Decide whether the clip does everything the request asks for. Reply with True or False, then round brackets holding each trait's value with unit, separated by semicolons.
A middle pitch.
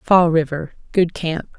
True (165 Hz)